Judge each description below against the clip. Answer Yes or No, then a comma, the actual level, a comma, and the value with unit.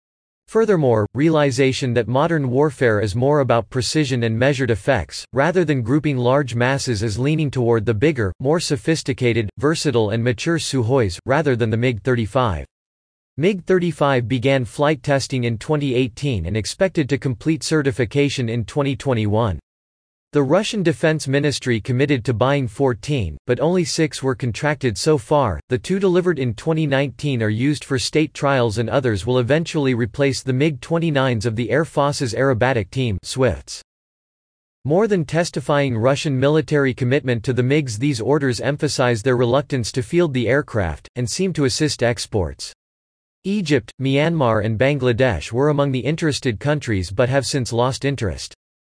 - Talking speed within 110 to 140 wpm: No, fast, 150 wpm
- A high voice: No, low, 135 Hz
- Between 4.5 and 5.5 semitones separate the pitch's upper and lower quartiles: No, average, 3.7 semitones